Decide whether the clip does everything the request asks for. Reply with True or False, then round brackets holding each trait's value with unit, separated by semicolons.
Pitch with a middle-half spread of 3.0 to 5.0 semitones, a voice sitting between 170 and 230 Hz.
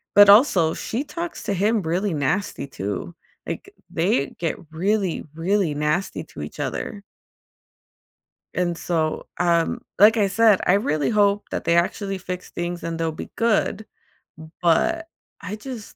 True (4.0 semitones; 185 Hz)